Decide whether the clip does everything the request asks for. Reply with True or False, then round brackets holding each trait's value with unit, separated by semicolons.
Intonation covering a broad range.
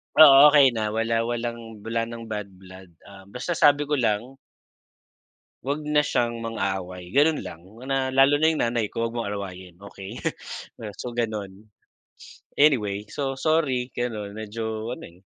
False (4.8 semitones)